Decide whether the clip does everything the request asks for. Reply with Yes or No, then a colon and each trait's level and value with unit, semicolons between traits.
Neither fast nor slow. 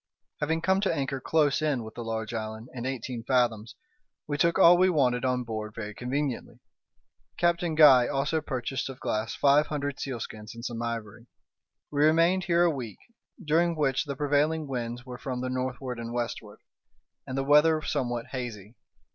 Yes: average, 170 wpm